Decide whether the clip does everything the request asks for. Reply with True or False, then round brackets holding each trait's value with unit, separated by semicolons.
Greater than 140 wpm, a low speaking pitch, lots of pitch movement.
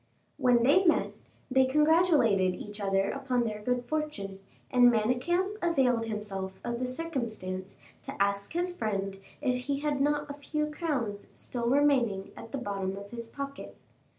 False (155 wpm; 245 Hz; 6.0 semitones)